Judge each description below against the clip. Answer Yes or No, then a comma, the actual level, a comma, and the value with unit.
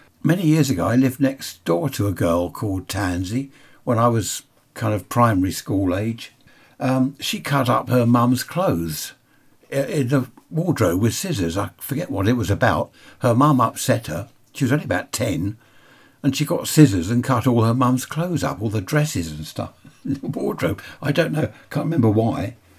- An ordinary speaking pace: Yes, average, 190 wpm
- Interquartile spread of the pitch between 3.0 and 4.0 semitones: No, average, 4.6 semitones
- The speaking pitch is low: Yes, low, 125 Hz